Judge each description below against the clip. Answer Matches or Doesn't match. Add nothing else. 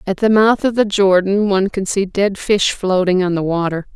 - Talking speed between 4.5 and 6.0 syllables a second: Matches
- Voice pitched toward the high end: Matches